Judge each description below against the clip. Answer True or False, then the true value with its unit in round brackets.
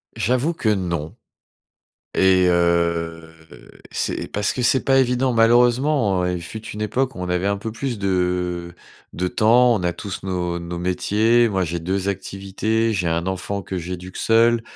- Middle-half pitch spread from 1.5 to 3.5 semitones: False (4.3 semitones)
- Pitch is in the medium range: False (95 Hz)